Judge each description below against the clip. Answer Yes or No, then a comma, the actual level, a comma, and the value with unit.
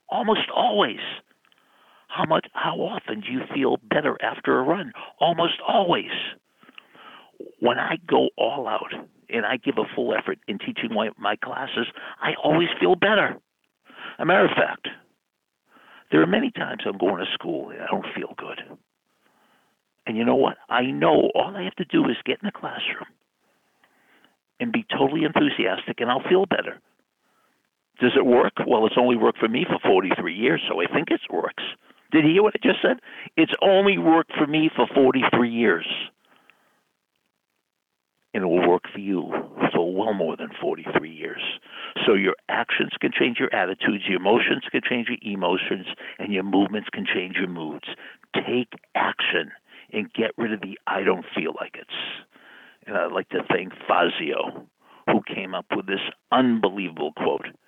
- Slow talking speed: No, average, 175 wpm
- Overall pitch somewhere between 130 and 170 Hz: Yes, low, 135 Hz